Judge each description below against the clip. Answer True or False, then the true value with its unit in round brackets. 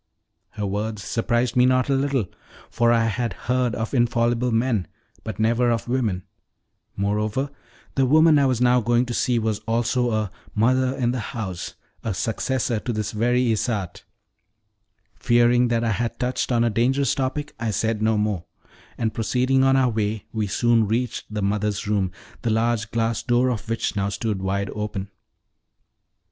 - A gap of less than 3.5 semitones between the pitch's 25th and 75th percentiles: True (2.6 semitones)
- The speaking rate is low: False (170 wpm)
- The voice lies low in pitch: True (115 Hz)